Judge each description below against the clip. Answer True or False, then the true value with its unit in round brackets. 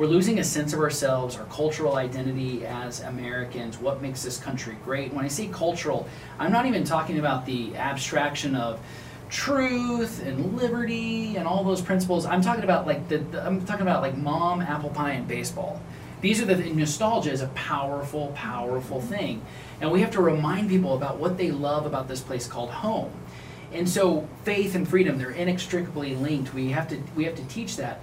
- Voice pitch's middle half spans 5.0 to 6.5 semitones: True (5.4 semitones)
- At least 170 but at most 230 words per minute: True (190 wpm)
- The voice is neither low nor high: True (150 Hz)